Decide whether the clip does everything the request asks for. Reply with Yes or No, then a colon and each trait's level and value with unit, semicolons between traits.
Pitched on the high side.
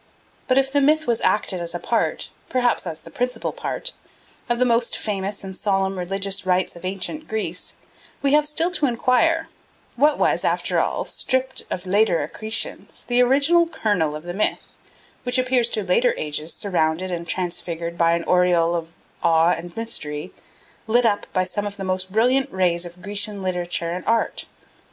Yes: high, 200 Hz